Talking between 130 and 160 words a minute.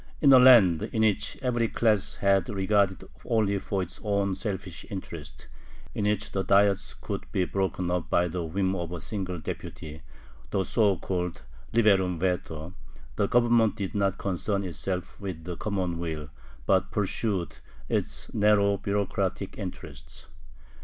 Yes: average, 145 wpm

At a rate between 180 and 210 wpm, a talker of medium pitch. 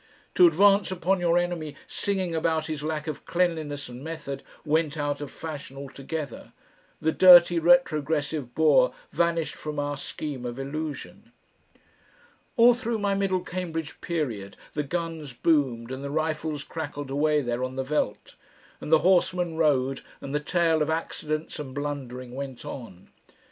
No: average, 150 wpm; medium, 155 Hz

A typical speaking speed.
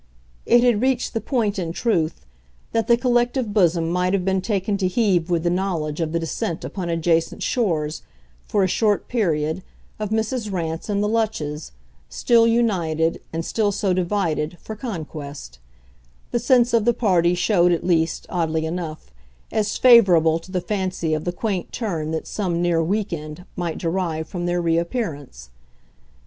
Yes: average, 165 wpm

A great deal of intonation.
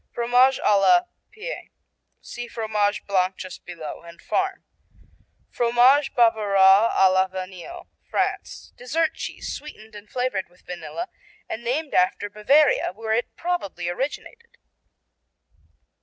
Yes: wide, 6.0 semitones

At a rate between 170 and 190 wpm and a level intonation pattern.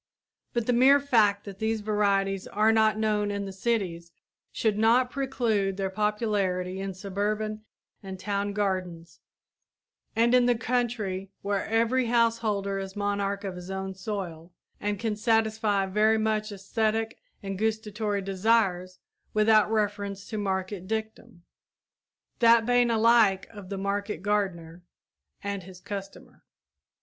No: slow, 135 wpm; narrow, 2.3 semitones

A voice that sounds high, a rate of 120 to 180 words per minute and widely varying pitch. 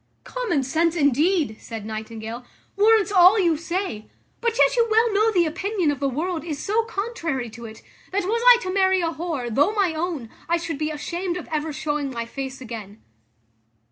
No: very high, 330 Hz; average, 190 wpm; wide, 6.5 semitones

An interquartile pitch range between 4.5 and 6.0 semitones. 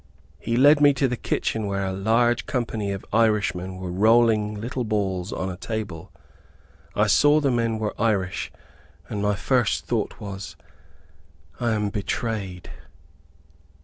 No: average, 3.3 semitones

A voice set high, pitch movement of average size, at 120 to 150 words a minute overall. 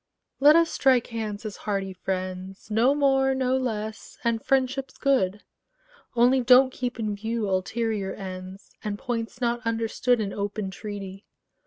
Yes: high, 225 Hz; average, 4.0 semitones; average, 145 wpm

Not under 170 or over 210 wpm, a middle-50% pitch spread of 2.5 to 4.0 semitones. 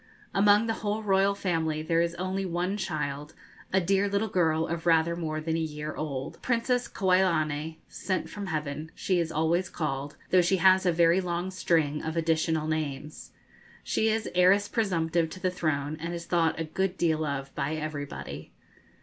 Yes: average, 175 wpm; average, 3.3 semitones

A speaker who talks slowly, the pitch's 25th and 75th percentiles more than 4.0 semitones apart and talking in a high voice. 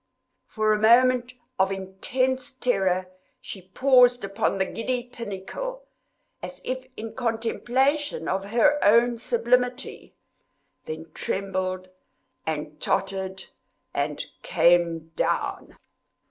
Yes: slow, 95 wpm; average, 4.8 semitones; high, 225 Hz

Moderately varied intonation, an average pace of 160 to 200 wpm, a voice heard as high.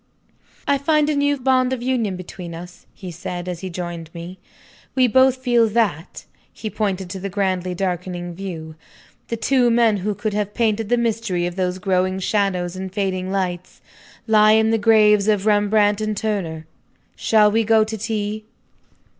Yes: average, 3.5 semitones; average, 170 wpm; high, 205 Hz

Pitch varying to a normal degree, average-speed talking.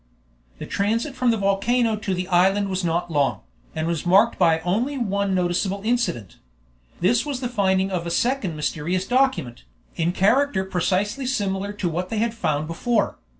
Yes: average, 4.7 semitones; average, 170 wpm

